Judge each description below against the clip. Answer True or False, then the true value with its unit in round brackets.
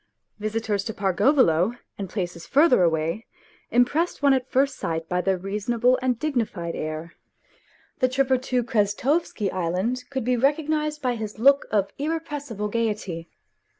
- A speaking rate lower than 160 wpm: True (140 wpm)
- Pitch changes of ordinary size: False (5.7 semitones)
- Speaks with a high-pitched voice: True (230 Hz)